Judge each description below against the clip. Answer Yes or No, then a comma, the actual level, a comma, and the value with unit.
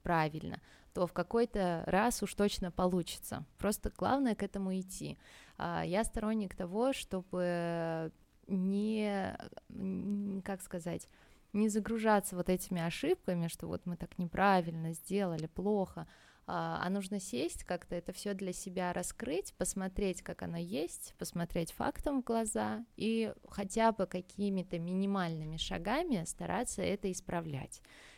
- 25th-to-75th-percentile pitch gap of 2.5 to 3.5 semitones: Yes, average, 2.8 semitones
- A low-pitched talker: No, high, 190 Hz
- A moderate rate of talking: Yes, average, 125 wpm